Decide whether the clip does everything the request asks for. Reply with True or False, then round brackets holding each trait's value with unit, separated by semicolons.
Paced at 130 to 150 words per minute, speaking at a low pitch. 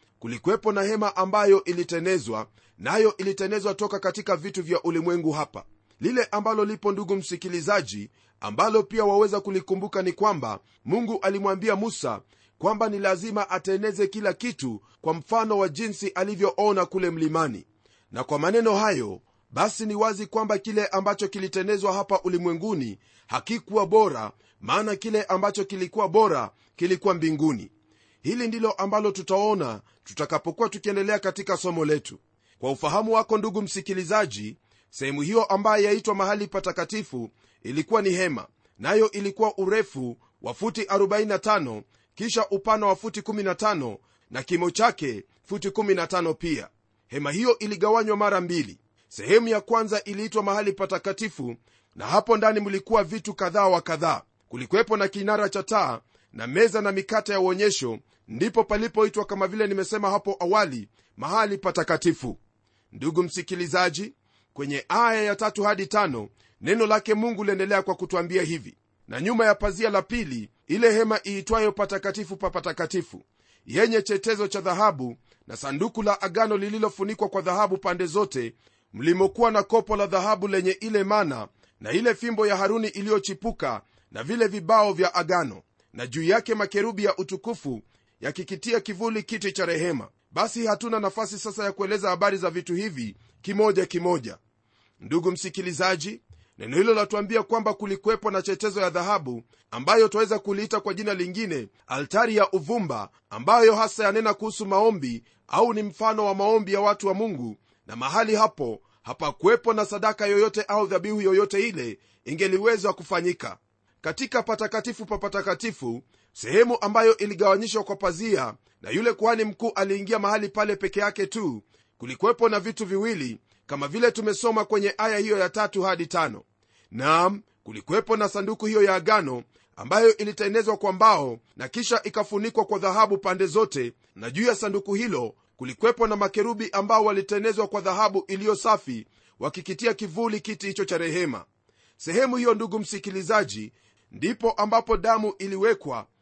False (140 wpm; 200 Hz)